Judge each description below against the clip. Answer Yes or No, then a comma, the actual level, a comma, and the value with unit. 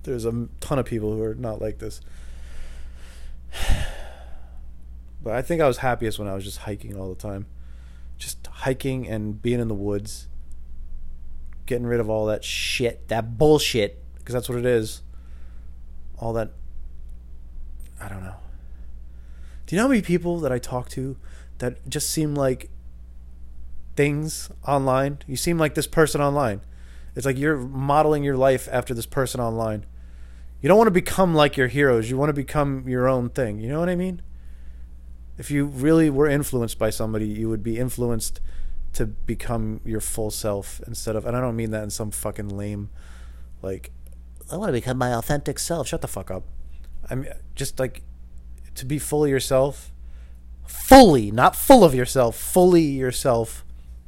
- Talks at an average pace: Yes, average, 175 wpm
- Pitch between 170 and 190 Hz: No, low, 110 Hz